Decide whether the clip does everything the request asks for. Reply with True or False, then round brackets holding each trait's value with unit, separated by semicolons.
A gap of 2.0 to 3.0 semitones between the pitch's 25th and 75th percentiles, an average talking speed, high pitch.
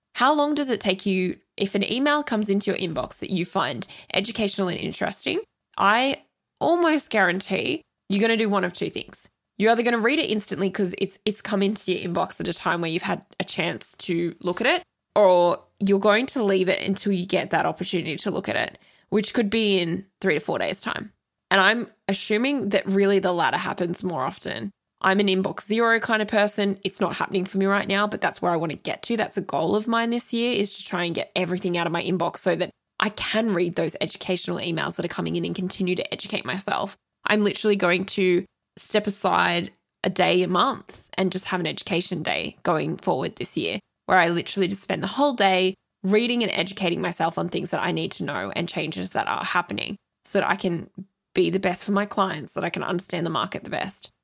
False (2.5 semitones; 230 wpm; 195 Hz)